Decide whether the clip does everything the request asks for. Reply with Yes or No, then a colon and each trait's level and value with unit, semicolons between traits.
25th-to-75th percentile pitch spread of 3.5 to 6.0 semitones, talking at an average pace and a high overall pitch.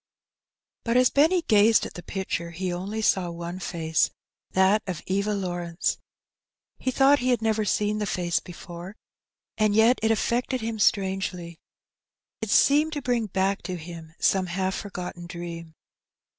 Yes: average, 4.1 semitones; average, 155 wpm; high, 195 Hz